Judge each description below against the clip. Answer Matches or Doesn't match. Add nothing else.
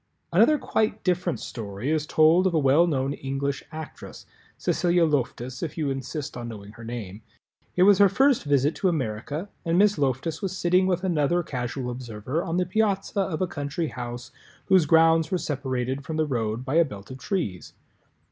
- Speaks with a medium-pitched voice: Matches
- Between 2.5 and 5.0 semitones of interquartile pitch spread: Doesn't match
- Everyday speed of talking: Matches